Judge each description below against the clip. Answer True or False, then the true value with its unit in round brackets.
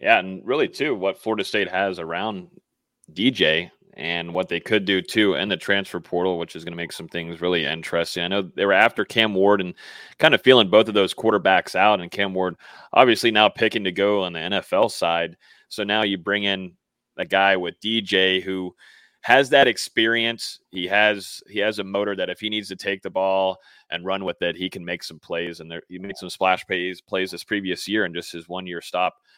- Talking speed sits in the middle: False (225 wpm)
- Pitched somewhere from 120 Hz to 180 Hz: False (95 Hz)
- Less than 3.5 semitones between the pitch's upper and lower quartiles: True (2.4 semitones)